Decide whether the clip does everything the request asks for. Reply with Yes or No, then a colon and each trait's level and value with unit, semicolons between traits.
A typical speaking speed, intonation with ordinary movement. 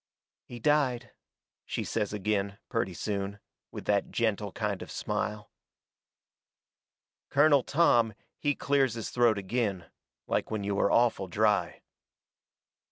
No: slow, 120 wpm; average, 3.1 semitones